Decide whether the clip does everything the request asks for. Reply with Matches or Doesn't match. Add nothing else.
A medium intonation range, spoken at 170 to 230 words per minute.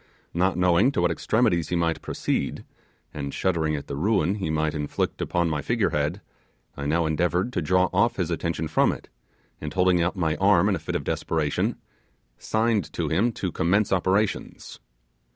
Matches